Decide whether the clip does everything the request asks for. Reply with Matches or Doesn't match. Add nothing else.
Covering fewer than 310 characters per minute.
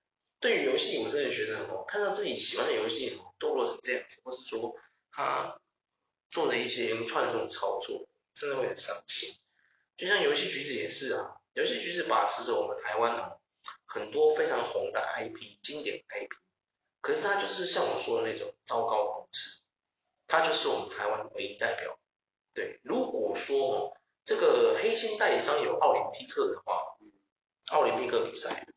Matches